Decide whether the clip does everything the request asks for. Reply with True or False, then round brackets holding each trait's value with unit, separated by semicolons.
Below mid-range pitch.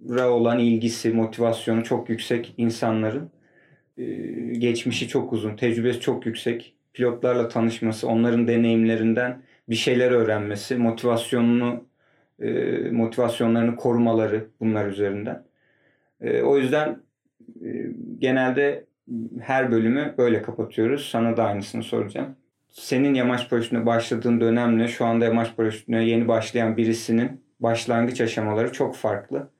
True (115 Hz)